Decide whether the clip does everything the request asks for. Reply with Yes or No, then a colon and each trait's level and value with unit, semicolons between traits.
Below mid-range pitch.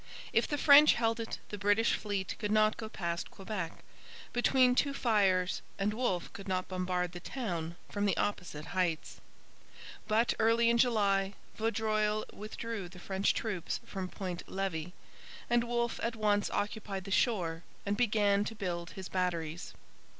No: high, 205 Hz